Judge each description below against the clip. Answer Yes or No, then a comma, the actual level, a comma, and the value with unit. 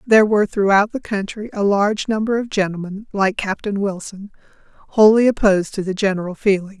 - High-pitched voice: Yes, high, 205 Hz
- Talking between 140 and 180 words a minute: Yes, average, 170 wpm